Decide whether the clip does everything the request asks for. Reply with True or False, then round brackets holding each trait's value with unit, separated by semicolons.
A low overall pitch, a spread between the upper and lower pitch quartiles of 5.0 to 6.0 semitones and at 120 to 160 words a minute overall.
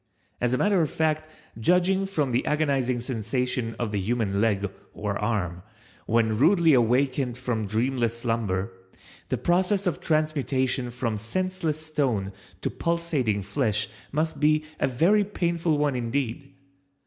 True (130 Hz; 5.5 semitones; 135 wpm)